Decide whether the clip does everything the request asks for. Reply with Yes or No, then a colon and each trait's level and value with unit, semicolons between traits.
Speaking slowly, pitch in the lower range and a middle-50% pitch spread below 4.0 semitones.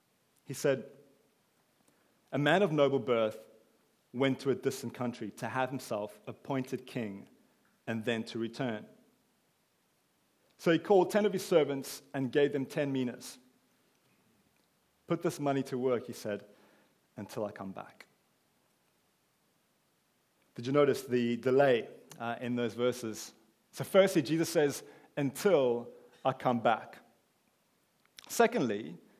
Yes: slow, 125 wpm; low, 130 Hz; average, 3.3 semitones